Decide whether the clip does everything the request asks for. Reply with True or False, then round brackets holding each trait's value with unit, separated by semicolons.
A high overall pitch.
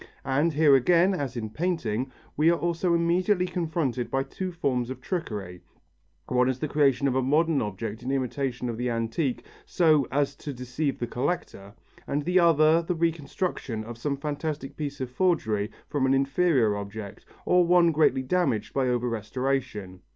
False (135 Hz)